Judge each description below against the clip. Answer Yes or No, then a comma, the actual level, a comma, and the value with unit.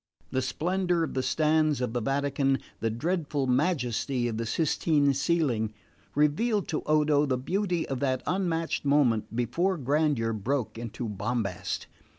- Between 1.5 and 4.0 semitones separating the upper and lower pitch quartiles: No, average, 4.7 semitones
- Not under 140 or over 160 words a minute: Yes, average, 145 wpm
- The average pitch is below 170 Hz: Yes, medium, 140 Hz